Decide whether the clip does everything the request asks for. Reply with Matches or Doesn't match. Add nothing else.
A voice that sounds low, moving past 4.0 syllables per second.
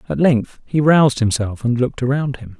Matches